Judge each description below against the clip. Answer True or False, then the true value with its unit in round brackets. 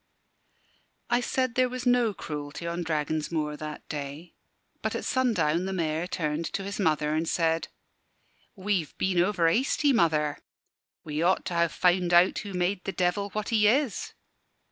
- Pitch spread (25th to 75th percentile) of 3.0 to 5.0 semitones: True (4.6 semitones)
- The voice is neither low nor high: True (175 Hz)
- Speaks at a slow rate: False (165 wpm)